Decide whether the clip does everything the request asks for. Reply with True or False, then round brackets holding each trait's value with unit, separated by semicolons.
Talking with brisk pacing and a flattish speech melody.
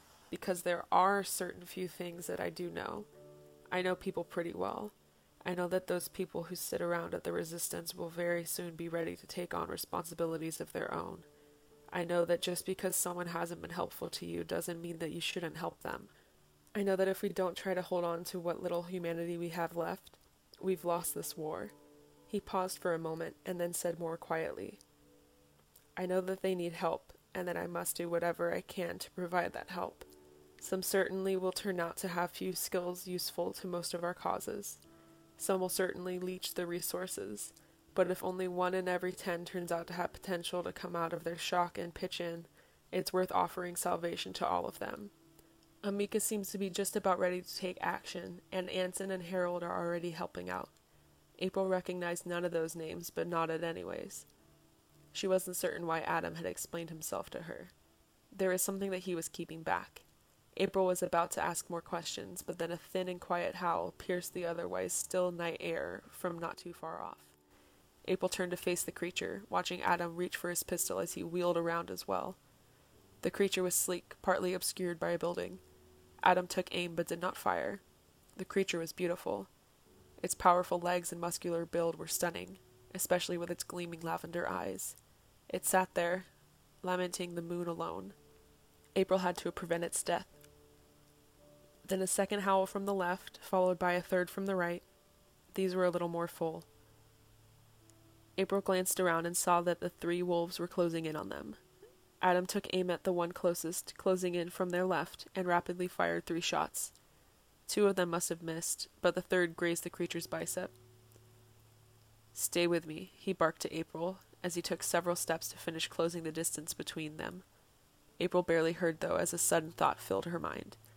False (190 wpm; 1.9 semitones)